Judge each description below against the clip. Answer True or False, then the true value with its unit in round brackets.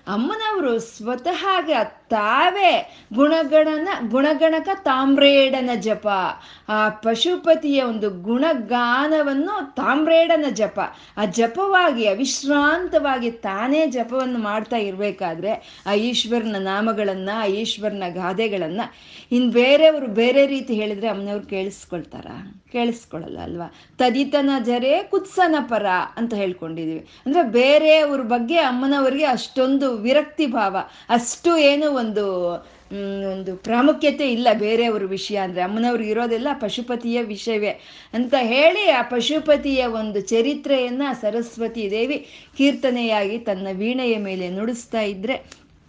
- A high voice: True (240 Hz)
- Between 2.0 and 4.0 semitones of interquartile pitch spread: False (5.3 semitones)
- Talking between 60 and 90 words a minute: False (100 wpm)